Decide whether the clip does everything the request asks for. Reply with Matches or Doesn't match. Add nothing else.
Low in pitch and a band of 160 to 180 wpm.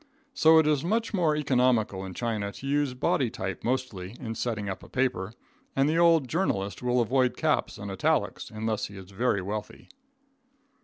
Matches